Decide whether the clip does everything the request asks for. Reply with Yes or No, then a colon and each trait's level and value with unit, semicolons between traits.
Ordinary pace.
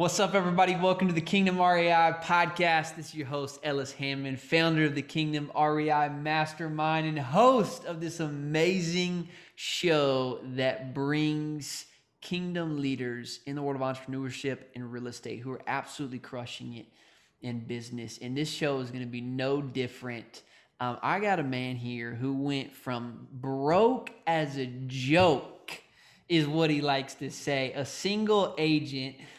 Yes: average, 155 wpm